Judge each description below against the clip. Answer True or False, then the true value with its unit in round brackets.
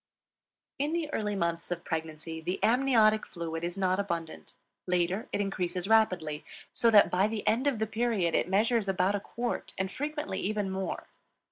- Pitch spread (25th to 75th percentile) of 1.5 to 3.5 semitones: False (4.2 semitones)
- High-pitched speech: True (195 Hz)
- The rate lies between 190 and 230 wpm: False (170 wpm)